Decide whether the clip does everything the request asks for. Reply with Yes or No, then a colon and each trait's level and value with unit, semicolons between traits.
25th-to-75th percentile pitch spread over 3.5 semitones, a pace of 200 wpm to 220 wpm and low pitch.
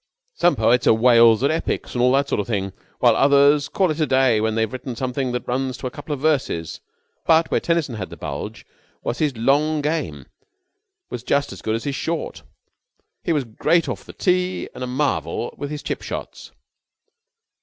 Yes: average, 4.4 semitones; fast, 205 wpm; low, 130 Hz